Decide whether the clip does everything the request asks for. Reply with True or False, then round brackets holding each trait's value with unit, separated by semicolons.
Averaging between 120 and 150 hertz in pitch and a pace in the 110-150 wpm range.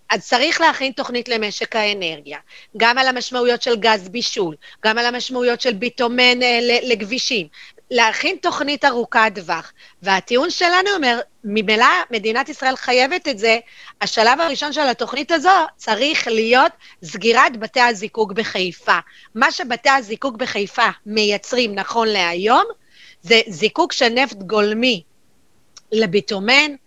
False (235 Hz; 125 wpm)